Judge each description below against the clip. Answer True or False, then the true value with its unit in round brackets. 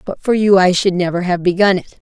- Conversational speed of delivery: False (255 wpm)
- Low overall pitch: False (185 Hz)